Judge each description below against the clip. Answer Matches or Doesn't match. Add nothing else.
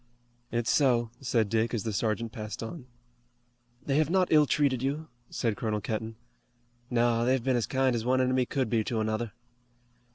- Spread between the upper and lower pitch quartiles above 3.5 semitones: Doesn't match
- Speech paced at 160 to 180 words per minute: Matches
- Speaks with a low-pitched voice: Matches